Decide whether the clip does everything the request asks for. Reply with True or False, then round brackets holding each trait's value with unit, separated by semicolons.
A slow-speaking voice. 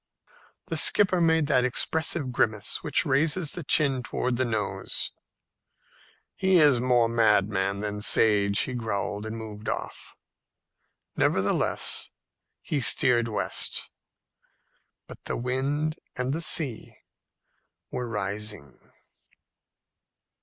True (105 wpm)